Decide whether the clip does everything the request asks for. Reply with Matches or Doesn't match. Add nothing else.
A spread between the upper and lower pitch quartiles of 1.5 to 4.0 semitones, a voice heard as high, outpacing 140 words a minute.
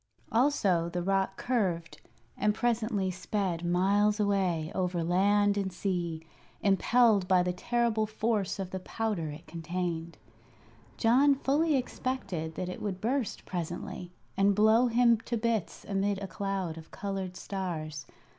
Doesn't match